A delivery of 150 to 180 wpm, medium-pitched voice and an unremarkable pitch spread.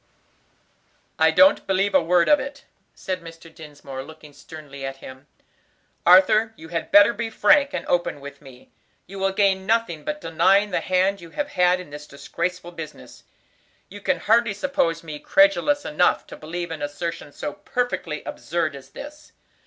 Yes: average, 170 wpm; medium, 180 Hz; average, 5.0 semitones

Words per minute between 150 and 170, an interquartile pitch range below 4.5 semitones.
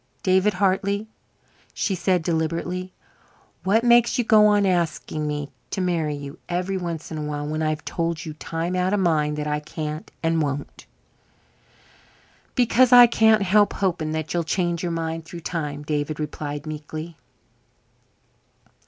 Yes: average, 155 wpm; average, 3.6 semitones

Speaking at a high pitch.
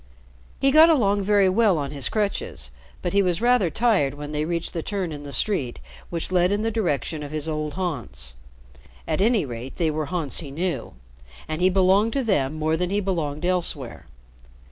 No: medium, 175 Hz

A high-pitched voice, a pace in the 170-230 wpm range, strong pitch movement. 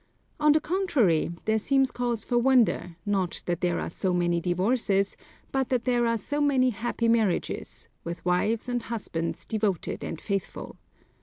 No: high, 225 Hz; average, 160 wpm; wide, 5.7 semitones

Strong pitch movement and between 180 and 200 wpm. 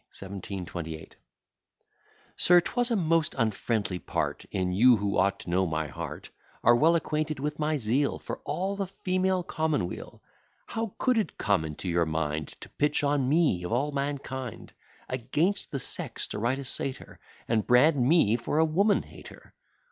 No: wide, 8.2 semitones; average, 165 wpm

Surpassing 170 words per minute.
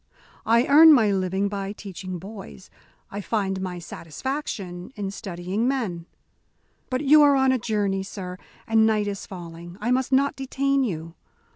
No: average, 155 wpm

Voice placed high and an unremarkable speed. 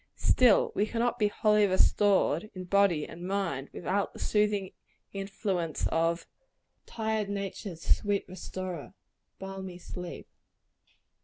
No: high, 195 Hz; slow, 110 wpm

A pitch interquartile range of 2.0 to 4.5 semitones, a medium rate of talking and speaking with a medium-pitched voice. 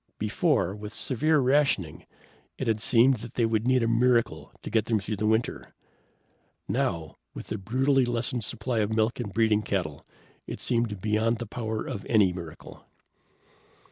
No: narrow, 2.6 semitones; average, 165 wpm; low, 110 Hz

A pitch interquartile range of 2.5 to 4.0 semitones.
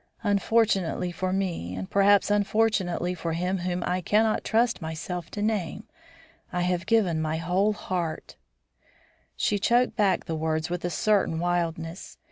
Yes: average, 3.5 semitones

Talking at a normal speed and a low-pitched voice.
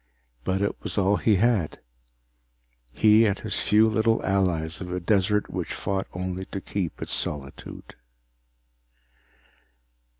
No: slow, 130 wpm; very low, 95 Hz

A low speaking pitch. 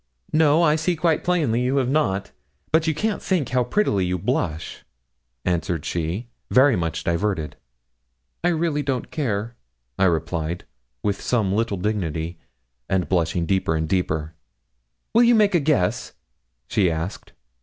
Yes: low, 105 Hz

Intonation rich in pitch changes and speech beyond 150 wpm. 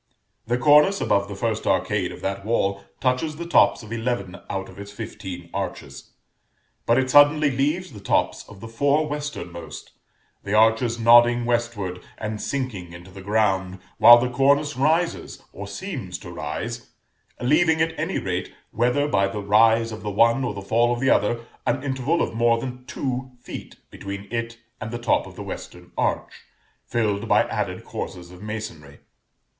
No: average, 4.7 semitones; average, 170 wpm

